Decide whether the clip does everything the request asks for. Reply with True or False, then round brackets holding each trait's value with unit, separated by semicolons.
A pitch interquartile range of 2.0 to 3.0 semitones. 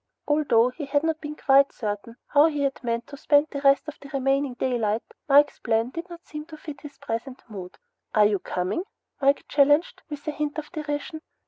False (3.6 semitones)